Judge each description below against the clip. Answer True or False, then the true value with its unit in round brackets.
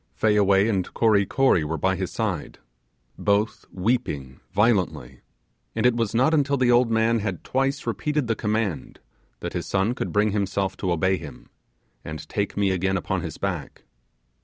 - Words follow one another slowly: False (165 wpm)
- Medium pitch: False (100 Hz)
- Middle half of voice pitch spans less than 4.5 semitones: True (3.6 semitones)